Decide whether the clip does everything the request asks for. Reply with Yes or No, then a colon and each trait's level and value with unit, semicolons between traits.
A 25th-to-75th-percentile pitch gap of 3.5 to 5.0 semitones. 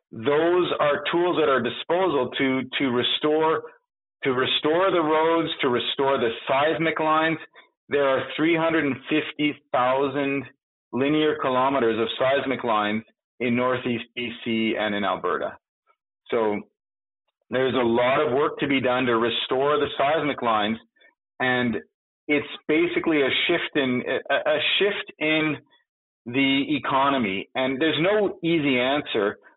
Yes: average, 4.0 semitones